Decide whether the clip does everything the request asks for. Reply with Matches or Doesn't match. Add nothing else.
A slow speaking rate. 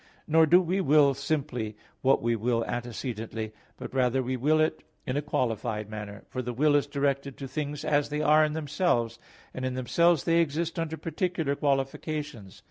Doesn't match